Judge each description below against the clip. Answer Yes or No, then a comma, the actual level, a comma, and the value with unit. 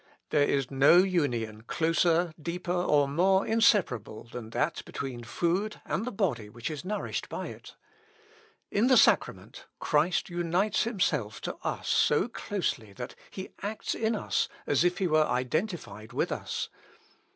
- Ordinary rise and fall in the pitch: No, wide, 7.0 semitones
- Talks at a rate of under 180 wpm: Yes, average, 150 wpm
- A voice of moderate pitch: Yes, medium, 165 Hz